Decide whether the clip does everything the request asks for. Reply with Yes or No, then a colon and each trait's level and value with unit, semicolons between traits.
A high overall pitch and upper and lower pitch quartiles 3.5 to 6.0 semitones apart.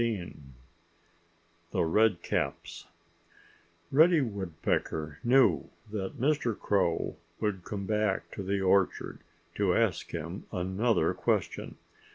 No: low, 100 Hz; average, 3.8 semitones